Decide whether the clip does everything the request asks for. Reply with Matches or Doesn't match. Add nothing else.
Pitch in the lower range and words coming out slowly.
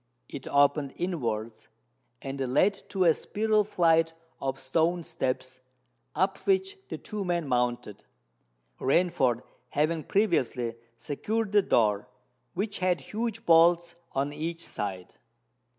Doesn't match